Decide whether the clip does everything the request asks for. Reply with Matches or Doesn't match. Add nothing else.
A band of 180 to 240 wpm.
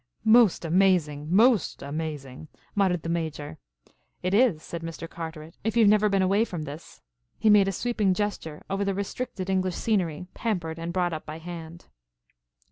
Doesn't match